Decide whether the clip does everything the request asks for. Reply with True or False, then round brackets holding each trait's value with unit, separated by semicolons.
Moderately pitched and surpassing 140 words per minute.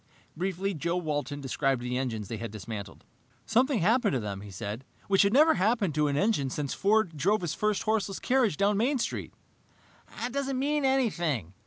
True (180 Hz; 190 wpm)